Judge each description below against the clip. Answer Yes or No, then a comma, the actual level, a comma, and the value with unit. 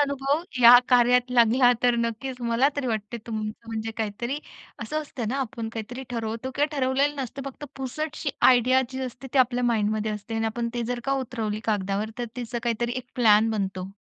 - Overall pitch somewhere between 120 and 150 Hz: No, high, 240 Hz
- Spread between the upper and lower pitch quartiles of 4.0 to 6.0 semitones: No, average, 2.8 semitones